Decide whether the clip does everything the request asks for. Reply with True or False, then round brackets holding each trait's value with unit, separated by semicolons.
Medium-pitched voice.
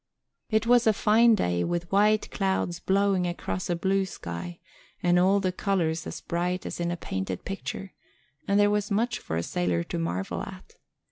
True (180 Hz)